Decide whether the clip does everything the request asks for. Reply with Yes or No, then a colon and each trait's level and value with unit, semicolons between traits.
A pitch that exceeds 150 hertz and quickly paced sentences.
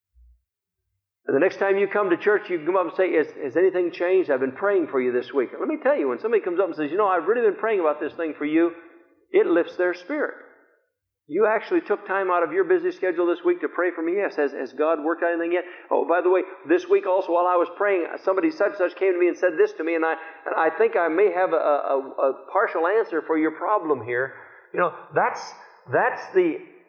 Yes: medium, 185 Hz; fast, 260 wpm